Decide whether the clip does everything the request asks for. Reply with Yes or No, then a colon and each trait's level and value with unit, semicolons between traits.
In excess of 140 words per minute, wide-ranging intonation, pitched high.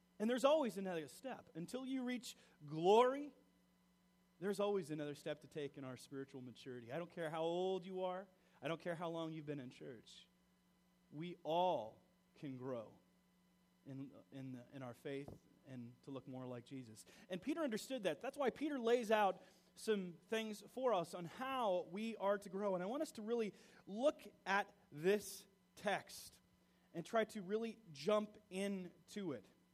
No: average, 175 wpm; wide, 7.0 semitones; medium, 180 Hz